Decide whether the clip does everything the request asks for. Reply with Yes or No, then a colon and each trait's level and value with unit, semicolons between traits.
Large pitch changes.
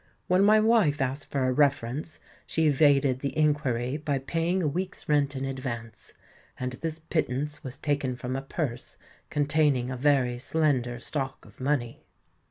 No: average, 3.0 semitones